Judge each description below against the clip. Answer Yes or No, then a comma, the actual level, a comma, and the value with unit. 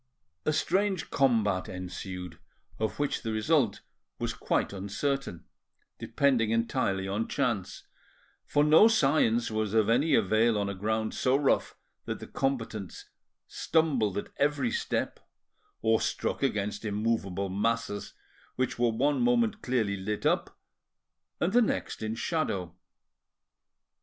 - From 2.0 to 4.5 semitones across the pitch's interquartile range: No, wide, 5.5 semitones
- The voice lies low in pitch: Yes, low, 115 Hz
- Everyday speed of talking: No, slow, 125 wpm